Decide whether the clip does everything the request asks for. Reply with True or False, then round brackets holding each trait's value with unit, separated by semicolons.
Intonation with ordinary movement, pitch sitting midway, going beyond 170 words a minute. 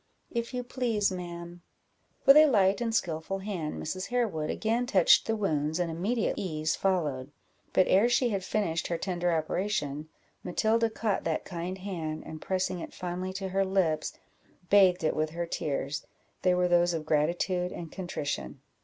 False (3.9 semitones; 180 Hz; 165 wpm)